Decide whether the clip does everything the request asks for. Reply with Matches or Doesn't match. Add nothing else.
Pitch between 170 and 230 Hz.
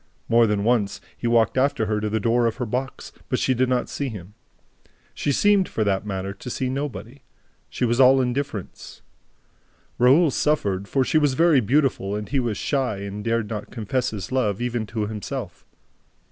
Doesn't match